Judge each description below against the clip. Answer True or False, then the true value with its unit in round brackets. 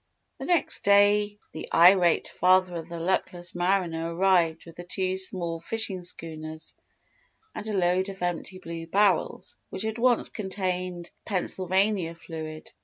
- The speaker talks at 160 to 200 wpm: False (135 wpm)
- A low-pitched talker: False (180 Hz)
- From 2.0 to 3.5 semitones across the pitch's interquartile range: True (2.6 semitones)